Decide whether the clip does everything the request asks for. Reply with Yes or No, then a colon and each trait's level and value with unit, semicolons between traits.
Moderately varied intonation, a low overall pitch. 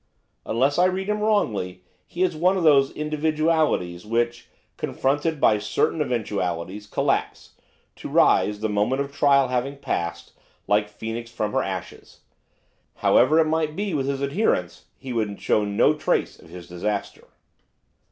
No: wide, 6.8 semitones; low, 130 Hz